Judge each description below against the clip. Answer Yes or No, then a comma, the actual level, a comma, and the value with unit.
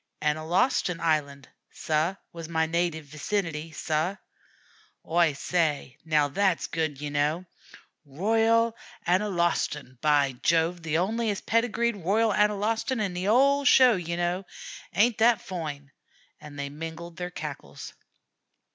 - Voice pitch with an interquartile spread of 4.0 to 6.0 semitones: Yes, average, 5.0 semitones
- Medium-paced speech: No, slow, 120 wpm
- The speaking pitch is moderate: Yes, medium, 170 Hz